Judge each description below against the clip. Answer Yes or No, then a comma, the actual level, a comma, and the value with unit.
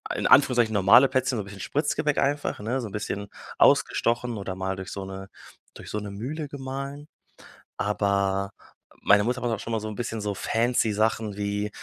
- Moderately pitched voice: No, low, 110 Hz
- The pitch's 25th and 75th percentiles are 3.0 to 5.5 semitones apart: Yes, average, 4.0 semitones